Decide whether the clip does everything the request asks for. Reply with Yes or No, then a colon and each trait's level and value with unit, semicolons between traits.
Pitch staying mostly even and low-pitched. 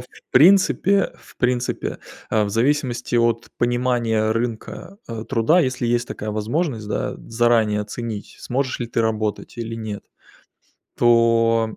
Yes: narrow, 2.0 semitones; low, 115 Hz